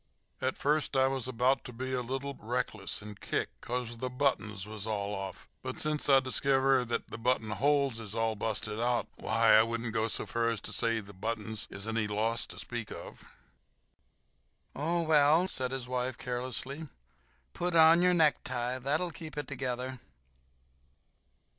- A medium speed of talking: Yes, average, 165 wpm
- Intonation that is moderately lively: Yes, average, 3.5 semitones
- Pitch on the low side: Yes, low, 125 Hz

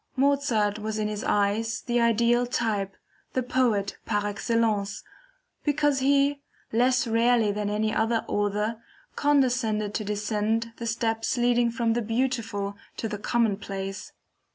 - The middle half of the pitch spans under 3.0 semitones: Yes, narrow, 2.6 semitones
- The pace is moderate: No, slow, 130 wpm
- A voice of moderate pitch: No, high, 225 Hz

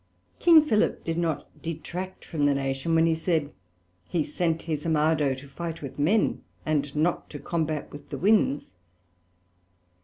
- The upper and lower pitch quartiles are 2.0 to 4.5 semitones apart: Yes, average, 2.8 semitones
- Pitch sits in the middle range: Yes, medium, 160 Hz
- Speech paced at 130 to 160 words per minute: Yes, average, 155 wpm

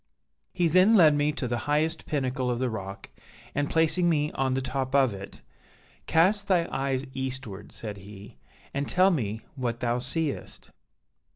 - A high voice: No, low, 135 Hz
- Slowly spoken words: No, average, 165 wpm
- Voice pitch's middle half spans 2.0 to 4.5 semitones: No, average, 5.0 semitones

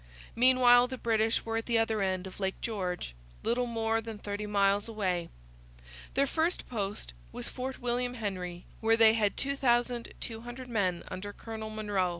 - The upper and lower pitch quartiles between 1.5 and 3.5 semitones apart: Yes, average, 3.1 semitones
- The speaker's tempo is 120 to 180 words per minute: Yes, average, 155 wpm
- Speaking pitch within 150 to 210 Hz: No, high, 225 Hz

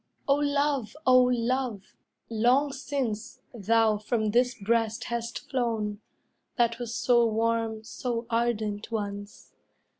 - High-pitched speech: Yes, high, 230 Hz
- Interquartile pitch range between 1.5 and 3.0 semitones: Yes, narrow, 2.4 semitones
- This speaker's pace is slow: Yes, slow, 115 wpm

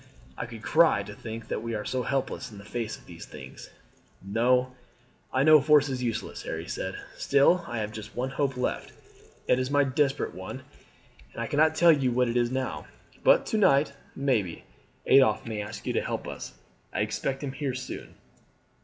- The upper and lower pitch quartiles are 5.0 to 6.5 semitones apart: No, average, 3.5 semitones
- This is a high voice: No, low, 130 Hz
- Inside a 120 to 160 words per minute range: No, average, 195 wpm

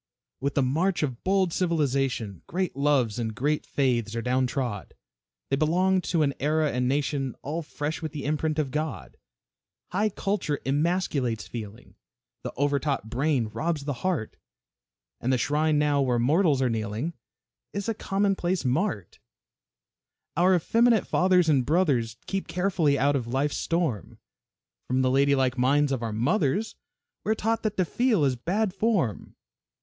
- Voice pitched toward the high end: No, medium, 145 Hz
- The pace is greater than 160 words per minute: No, average, 155 wpm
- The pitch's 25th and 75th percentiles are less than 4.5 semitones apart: No, wide, 5.5 semitones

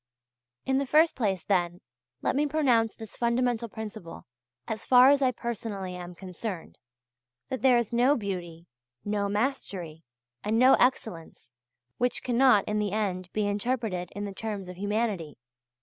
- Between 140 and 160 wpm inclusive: Yes, average, 150 wpm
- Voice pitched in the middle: No, high, 215 Hz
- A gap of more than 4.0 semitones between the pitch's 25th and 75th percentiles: Yes, average, 4.7 semitones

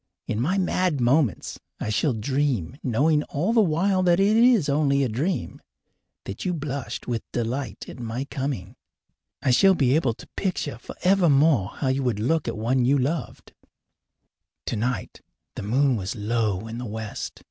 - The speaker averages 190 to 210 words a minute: No, average, 165 wpm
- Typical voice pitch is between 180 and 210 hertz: No, low, 135 Hz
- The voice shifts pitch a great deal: Yes, wide, 5.8 semitones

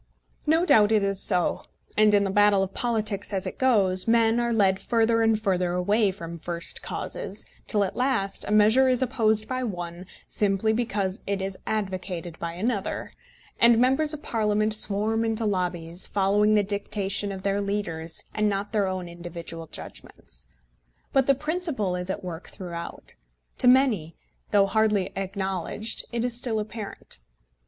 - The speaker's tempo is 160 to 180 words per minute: Yes, average, 165 wpm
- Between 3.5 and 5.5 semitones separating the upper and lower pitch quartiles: No, average, 3.1 semitones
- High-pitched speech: Yes, high, 205 Hz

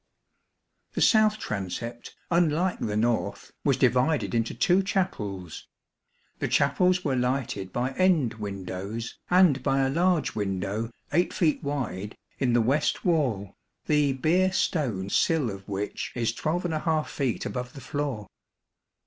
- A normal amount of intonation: No, wide, 6.9 semitones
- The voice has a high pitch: No, low, 130 Hz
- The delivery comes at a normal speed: No, slow, 130 wpm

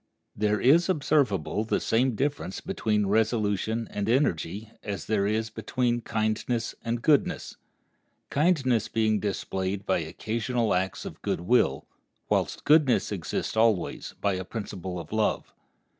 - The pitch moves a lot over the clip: No, average, 3.4 semitones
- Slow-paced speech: Yes, slow, 130 wpm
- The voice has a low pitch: Yes, low, 110 Hz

